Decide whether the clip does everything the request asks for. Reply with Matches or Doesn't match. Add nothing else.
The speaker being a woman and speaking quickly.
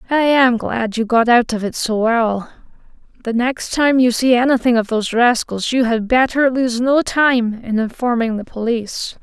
Doesn't match